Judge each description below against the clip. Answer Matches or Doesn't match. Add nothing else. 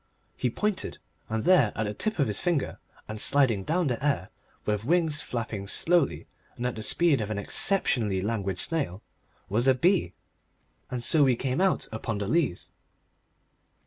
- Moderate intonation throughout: Doesn't match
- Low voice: Matches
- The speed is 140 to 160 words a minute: Doesn't match